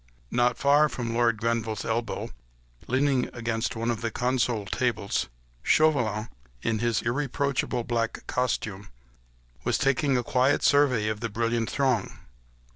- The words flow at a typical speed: No, slow, 130 wpm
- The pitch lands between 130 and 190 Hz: No, low, 120 Hz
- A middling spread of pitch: No, narrow, 2.3 semitones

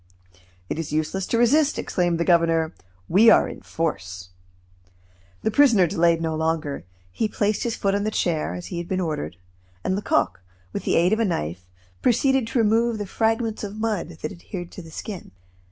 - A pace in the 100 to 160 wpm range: No, average, 185 wpm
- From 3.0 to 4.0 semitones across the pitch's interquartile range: No, average, 5.2 semitones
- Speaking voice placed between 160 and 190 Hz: Yes, medium, 185 Hz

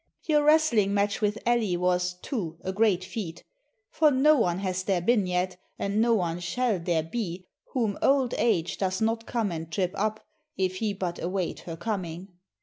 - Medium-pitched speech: No, high, 195 Hz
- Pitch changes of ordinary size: Yes, average, 4.1 semitones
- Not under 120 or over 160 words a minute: No, average, 180 wpm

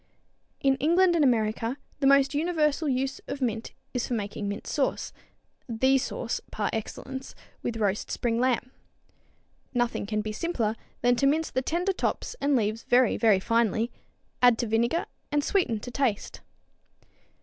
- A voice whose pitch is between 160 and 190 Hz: No, very high, 250 Hz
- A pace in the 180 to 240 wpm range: No, average, 155 wpm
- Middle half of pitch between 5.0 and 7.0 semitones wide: No, average, 3.9 semitones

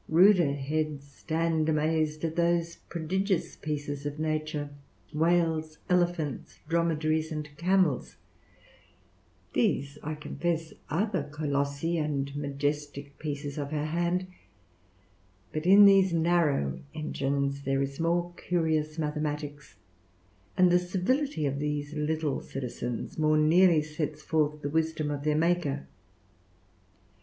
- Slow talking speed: Yes, slow, 115 wpm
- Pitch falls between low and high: Yes, medium, 155 Hz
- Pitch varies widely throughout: No, narrow, 2.5 semitones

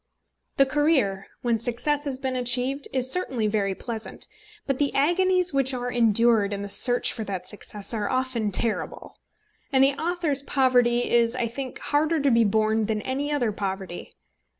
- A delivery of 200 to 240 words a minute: No, average, 170 wpm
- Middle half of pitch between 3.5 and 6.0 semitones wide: Yes, average, 4.0 semitones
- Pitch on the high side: Yes, high, 245 Hz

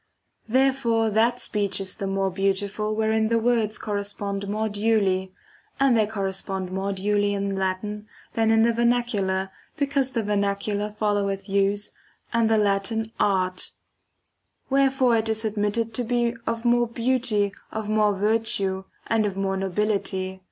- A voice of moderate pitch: No, high, 210 Hz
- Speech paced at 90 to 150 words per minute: Yes, average, 145 wpm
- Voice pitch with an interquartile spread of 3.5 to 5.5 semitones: No, narrow, 2.4 semitones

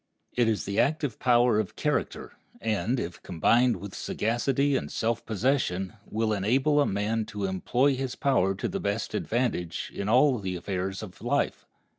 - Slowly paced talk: No, average, 165 wpm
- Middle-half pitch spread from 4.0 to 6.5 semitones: Yes, average, 4.4 semitones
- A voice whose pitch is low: Yes, low, 110 Hz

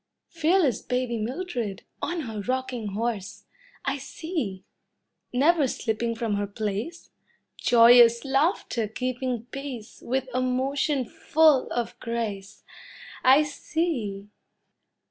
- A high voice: Yes, very high, 250 Hz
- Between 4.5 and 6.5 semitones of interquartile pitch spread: No, average, 3.8 semitones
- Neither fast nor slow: No, slow, 105 wpm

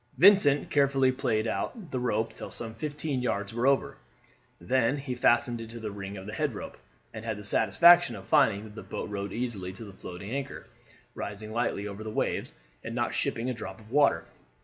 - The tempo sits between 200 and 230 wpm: Yes, fast, 205 wpm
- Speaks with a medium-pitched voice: No, low, 115 Hz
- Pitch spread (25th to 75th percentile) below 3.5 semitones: No, average, 4.3 semitones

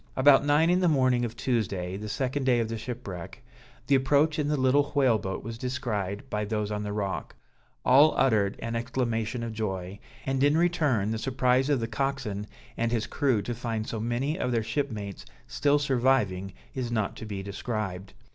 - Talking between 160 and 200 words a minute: Yes, average, 190 wpm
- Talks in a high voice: No, low, 120 Hz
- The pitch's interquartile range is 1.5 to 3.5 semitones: No, average, 4.1 semitones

